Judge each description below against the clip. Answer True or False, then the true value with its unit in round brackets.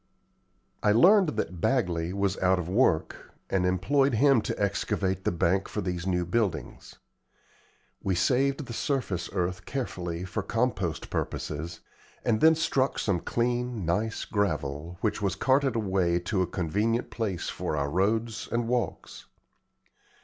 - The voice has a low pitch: True (100 Hz)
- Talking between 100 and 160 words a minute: True (140 wpm)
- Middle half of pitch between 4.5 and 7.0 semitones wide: True (5.0 semitones)